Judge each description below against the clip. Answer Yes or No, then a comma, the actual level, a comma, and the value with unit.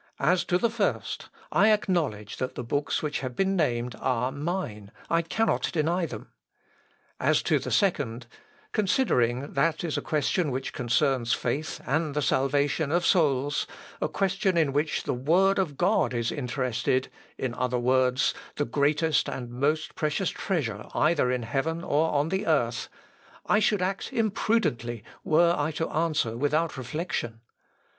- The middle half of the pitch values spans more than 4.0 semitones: Yes, average, 5.2 semitones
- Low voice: No, medium, 150 Hz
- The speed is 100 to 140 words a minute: No, average, 155 wpm